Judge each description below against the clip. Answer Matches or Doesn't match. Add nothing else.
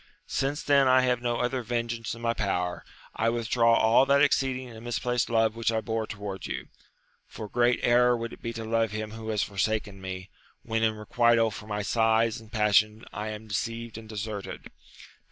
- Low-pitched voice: Matches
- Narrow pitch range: Matches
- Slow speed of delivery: Doesn't match